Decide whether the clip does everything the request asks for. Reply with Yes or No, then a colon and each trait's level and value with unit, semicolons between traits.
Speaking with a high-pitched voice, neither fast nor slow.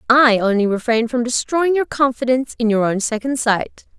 Yes: high, 240 Hz; average, 180 wpm